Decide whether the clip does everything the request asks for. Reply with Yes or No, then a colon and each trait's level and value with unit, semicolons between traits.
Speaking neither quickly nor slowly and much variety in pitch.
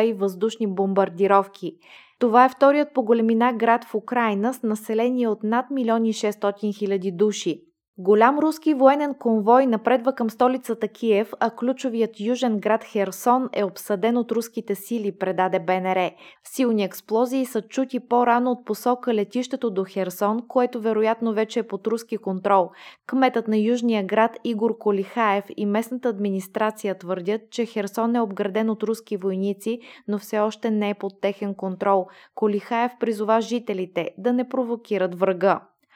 No: average, 145 wpm; average, 3.0 semitones